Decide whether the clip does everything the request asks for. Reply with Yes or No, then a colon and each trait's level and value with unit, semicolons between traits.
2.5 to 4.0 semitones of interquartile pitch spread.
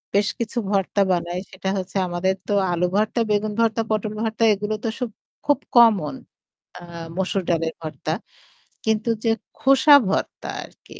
Yes: average, 3.6 semitones